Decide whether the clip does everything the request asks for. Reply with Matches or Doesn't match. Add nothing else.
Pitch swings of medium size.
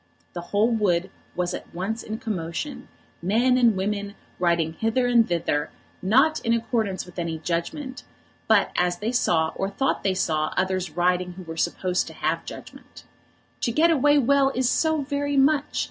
Doesn't match